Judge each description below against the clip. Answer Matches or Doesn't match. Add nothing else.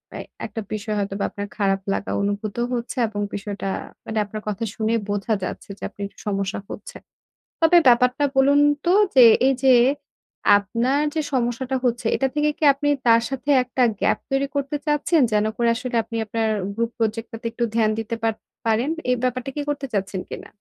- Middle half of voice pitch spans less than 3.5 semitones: Doesn't match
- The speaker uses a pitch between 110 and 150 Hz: Doesn't match